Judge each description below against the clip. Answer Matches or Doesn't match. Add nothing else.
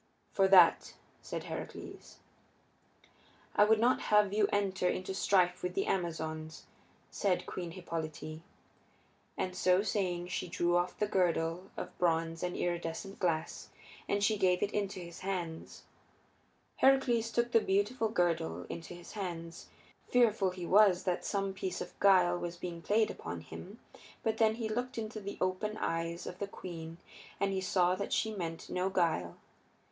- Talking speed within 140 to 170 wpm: Matches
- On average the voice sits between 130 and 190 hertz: Matches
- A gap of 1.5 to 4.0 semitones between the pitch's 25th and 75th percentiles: Matches